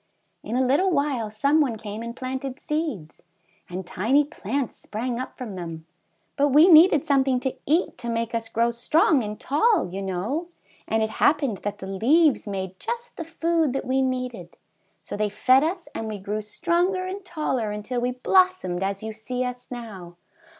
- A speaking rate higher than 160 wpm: Yes, average, 185 wpm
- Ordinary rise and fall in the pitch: No, wide, 6.0 semitones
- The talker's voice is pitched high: Yes, very high, 250 Hz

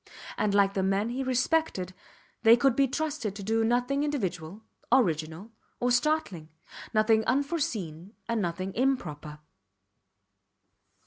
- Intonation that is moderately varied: No, wide, 5.7 semitones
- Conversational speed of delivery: No, slow, 120 wpm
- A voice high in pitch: Yes, high, 225 Hz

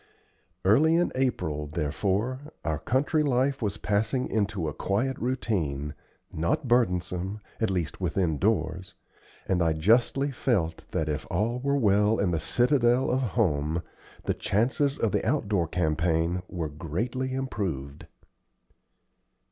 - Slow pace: Yes, slow, 130 wpm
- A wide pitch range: Yes, wide, 7.2 semitones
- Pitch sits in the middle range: No, low, 100 Hz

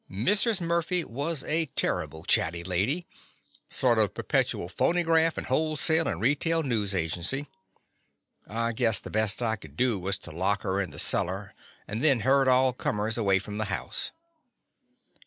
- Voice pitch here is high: No, low, 115 Hz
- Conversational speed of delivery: Yes, average, 160 wpm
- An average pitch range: No, wide, 7.7 semitones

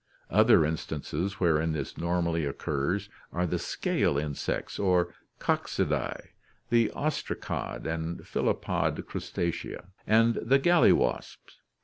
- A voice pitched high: No, very low, 85 Hz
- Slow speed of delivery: Yes, slow, 105 wpm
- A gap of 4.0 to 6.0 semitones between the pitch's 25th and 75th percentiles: Yes, average, 5.0 semitones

